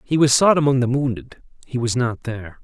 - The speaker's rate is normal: No, fast, 230 wpm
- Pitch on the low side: Yes, low, 125 Hz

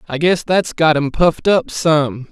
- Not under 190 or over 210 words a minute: Yes, fast, 205 wpm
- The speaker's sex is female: No, male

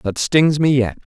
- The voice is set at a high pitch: No, low, 135 Hz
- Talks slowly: No, fast, 210 wpm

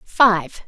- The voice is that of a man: No, female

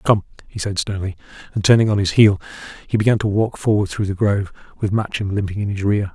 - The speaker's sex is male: Yes, male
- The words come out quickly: Yes, fast, 225 wpm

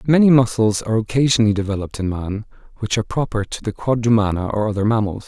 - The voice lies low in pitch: Yes, low, 110 Hz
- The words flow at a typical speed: Yes, average, 180 wpm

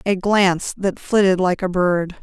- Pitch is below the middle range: No, medium, 185 Hz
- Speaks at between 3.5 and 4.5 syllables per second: Yes, 4.3 syllables/s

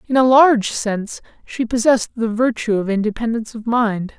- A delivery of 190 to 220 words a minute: No, average, 170 wpm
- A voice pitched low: No, high, 230 Hz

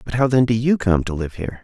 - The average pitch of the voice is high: No, low, 110 Hz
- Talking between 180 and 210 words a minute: No, fast, 330 wpm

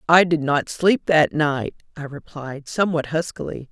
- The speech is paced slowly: No, average, 160 wpm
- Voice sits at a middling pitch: Yes, medium, 155 Hz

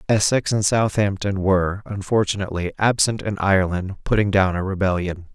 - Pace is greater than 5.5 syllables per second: No, 5.4 syllables/s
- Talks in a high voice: No, low, 100 Hz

